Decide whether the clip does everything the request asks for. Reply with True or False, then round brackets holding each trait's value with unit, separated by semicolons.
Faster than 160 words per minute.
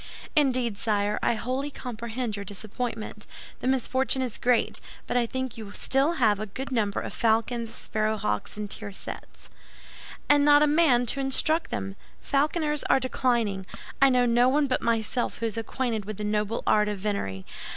True (170 wpm)